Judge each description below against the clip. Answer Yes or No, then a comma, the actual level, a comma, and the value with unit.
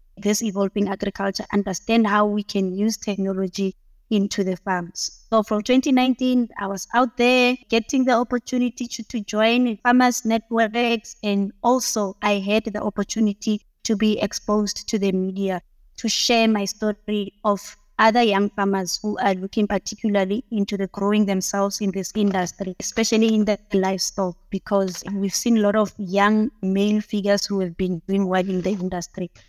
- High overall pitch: Yes, high, 205 Hz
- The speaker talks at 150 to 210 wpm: Yes, average, 160 wpm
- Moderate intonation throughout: No, narrow, 2.3 semitones